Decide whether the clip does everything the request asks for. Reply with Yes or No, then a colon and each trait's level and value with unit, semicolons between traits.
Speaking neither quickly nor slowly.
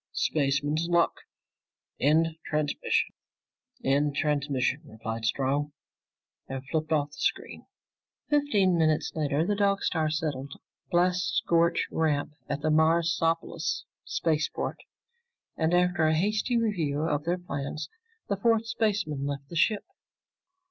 No: slow, 125 wpm